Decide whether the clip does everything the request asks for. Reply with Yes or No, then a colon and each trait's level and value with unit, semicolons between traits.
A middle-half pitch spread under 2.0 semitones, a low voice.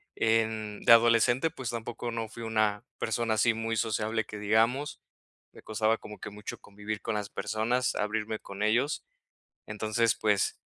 Yes: narrow, 1.5 semitones; low, 110 Hz